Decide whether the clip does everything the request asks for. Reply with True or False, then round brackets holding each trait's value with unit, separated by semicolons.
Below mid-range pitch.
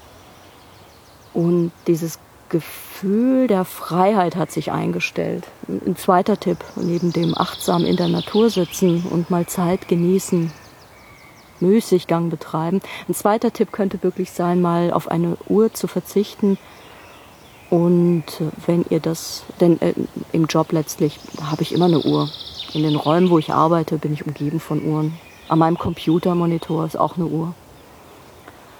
False (170 Hz)